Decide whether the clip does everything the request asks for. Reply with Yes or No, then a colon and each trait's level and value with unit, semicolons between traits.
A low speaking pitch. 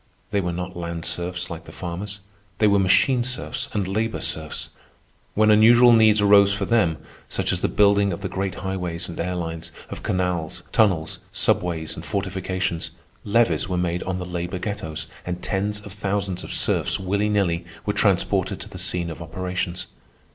Yes: very low, 95 Hz